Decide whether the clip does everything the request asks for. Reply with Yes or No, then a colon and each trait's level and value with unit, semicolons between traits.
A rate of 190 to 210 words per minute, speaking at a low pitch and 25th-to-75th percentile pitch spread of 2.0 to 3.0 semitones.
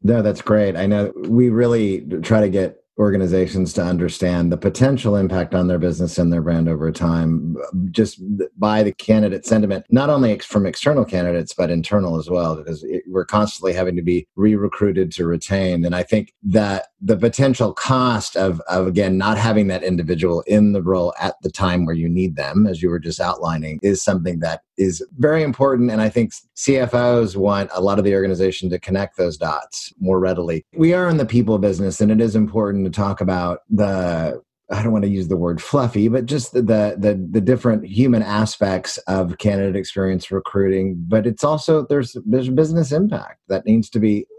No: average, 200 wpm; low, 100 Hz; average, 3.5 semitones